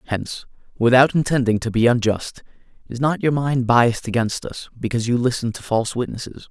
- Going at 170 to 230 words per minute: Yes, average, 175 wpm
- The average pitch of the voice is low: Yes, low, 120 Hz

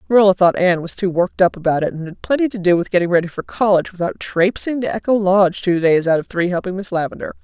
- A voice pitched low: No, medium, 185 Hz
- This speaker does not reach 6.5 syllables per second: No, 6.8 syllables/s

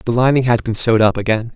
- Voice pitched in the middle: No, low, 115 Hz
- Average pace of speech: No, fast, 270 wpm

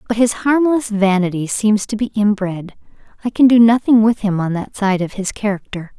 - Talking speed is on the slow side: No, average, 200 wpm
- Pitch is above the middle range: Yes, high, 210 Hz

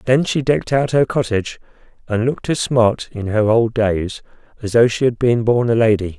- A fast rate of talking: Yes, fast, 215 wpm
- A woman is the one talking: No, male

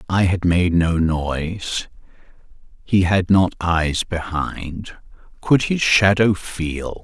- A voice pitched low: Yes, very low, 90 Hz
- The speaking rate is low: Yes, slow, 110 wpm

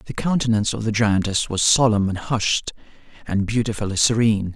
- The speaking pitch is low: Yes, low, 110 Hz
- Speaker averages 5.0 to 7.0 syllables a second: Yes, 5.7 syllables/s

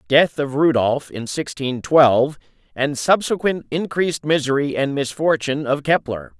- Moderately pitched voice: Yes, medium, 145 Hz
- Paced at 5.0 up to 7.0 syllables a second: No, 4.7 syllables/s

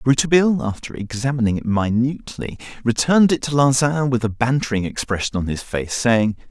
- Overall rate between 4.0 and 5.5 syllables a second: No, 5.8 syllables/s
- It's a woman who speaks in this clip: No, male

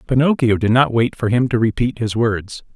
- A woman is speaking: No, male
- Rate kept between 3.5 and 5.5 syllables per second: Yes, 5.1 syllables/s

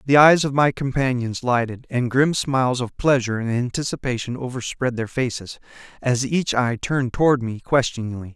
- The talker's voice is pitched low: Yes, low, 125 Hz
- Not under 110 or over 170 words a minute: Yes, average, 165 wpm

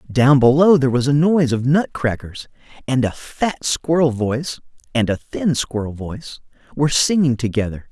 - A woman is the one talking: No, male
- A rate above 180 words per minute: No, average, 160 wpm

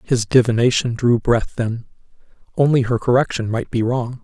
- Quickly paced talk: No, average, 155 wpm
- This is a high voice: No, low, 120 Hz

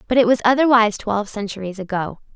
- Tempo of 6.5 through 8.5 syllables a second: Yes, 6.8 syllables/s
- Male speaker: No, female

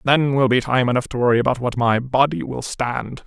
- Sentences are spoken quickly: Yes, fast, 240 wpm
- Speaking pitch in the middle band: No, low, 125 Hz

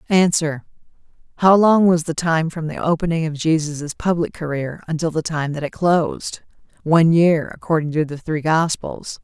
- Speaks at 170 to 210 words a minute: No, average, 155 wpm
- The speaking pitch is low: No, medium, 160 Hz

